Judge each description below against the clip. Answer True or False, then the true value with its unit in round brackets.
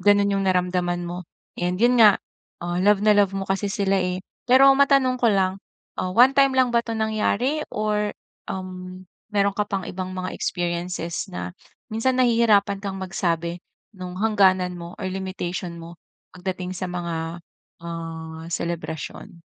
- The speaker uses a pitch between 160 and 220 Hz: True (190 Hz)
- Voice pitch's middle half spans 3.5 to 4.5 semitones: False (3.0 semitones)